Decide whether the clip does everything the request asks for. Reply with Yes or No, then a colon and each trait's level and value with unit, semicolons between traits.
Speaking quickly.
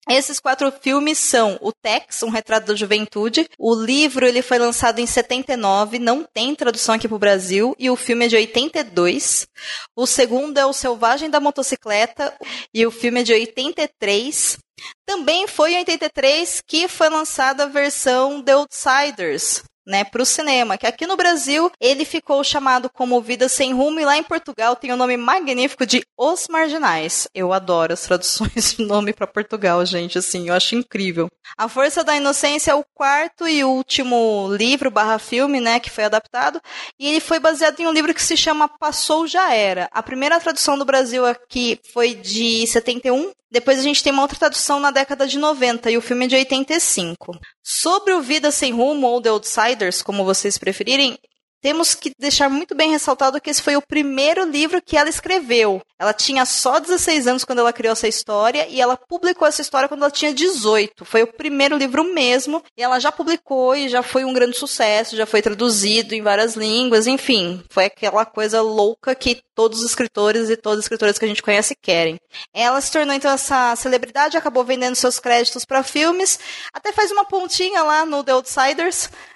Yes: fast, 190 wpm